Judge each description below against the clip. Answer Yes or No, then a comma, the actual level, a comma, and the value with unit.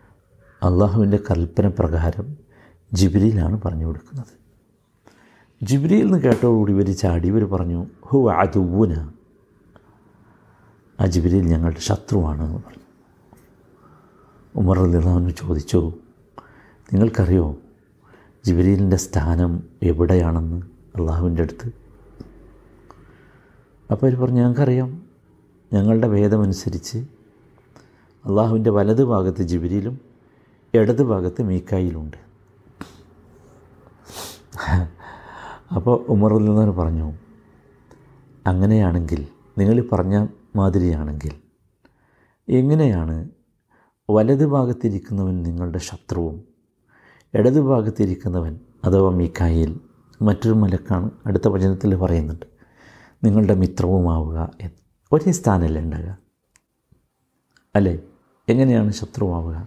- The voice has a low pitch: Yes, low, 100 Hz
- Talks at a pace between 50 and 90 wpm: Yes, average, 70 wpm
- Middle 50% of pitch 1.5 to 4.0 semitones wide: No, average, 4.4 semitones